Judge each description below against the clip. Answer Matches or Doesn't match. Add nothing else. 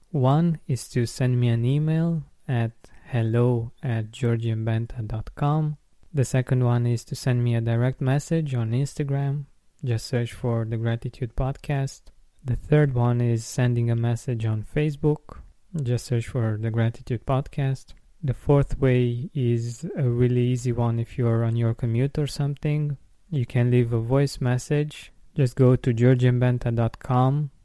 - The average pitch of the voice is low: Matches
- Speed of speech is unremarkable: Matches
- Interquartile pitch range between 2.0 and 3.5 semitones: Matches